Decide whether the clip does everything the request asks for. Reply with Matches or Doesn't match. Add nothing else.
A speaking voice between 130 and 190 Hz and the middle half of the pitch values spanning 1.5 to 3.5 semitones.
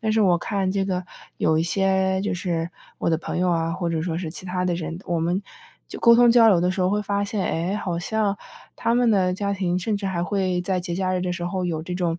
Matches